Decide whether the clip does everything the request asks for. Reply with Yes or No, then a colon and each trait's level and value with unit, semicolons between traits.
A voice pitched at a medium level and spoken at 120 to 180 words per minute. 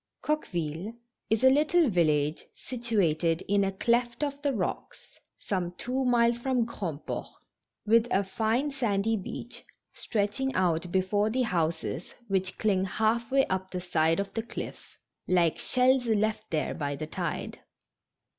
No: high, 210 Hz; average, 145 wpm